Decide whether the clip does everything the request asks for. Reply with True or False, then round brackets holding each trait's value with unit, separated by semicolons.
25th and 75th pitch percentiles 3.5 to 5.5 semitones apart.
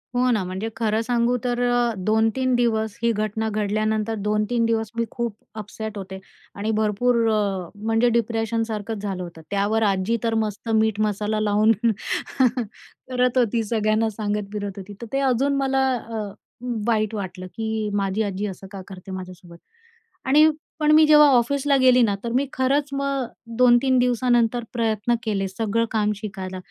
False (2.8 semitones)